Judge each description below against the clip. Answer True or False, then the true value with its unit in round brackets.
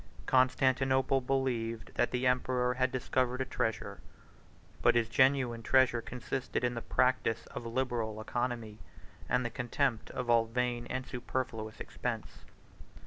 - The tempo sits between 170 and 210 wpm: False (135 wpm)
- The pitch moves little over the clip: True (1.9 semitones)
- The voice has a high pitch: False (125 Hz)